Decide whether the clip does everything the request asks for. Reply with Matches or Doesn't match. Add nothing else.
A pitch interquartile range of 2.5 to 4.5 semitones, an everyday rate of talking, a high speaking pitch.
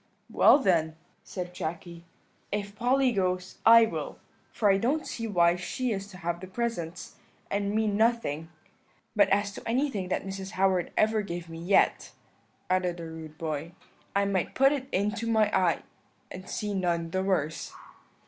Matches